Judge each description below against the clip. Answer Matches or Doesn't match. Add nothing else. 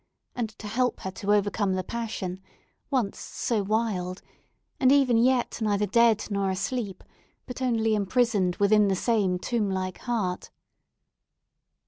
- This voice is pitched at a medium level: Doesn't match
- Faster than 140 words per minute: Doesn't match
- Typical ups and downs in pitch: Matches